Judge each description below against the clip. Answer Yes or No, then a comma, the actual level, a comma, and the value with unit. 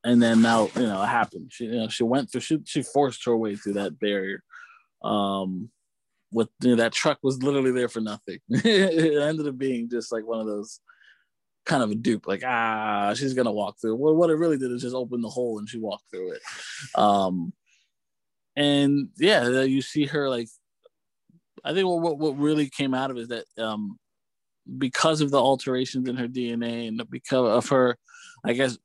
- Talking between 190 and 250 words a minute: Yes, fast, 205 wpm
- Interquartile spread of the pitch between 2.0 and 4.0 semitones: No, average, 4.5 semitones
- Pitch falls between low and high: No, low, 125 Hz